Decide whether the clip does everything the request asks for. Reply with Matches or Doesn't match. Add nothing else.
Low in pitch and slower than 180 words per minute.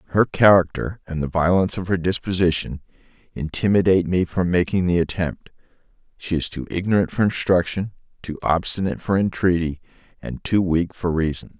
Matches